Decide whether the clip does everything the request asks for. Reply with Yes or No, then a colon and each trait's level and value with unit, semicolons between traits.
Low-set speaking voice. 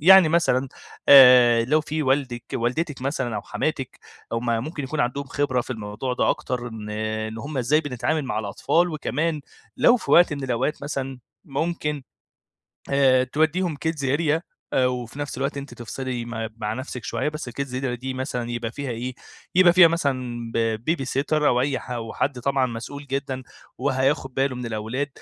Yes: low, 130 Hz